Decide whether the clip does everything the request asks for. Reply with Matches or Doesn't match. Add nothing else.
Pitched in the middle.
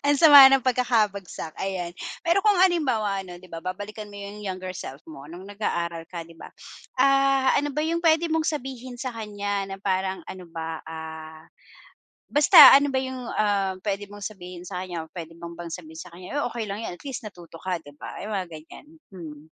Doesn't match